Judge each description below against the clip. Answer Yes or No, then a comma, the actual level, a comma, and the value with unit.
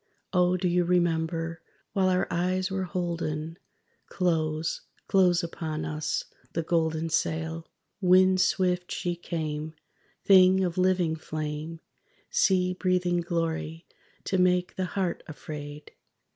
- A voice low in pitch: No, medium, 175 Hz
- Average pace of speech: No, slow, 115 wpm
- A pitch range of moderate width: No, narrow, 2.3 semitones